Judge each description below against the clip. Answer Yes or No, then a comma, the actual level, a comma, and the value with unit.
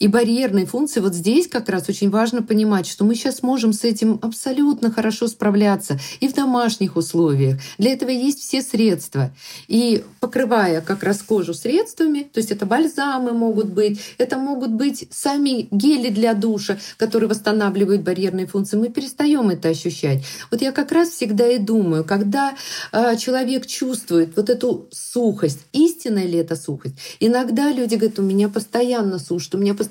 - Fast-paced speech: Yes, fast, 165 wpm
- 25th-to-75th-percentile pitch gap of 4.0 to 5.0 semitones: Yes, average, 4.4 semitones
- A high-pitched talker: Yes, high, 225 Hz